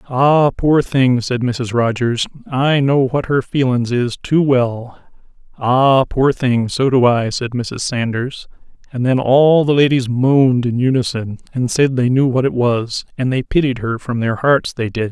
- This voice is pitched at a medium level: No, low, 125 Hz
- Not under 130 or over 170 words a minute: No, average, 185 wpm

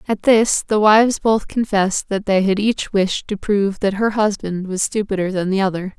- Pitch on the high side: Yes, high, 200 Hz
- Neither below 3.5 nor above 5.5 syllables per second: Yes, 5.0 syllables/s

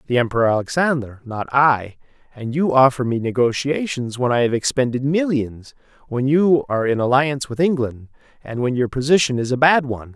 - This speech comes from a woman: No, male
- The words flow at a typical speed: Yes, average, 175 wpm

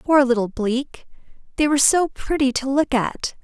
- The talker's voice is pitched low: No, very high, 270 Hz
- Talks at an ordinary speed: Yes, average, 175 wpm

